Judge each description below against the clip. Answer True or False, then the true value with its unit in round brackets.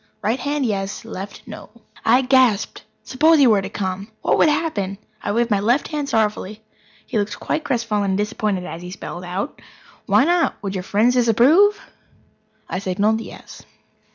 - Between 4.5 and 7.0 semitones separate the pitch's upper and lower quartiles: True (4.8 semitones)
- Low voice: False (220 Hz)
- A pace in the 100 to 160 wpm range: False (170 wpm)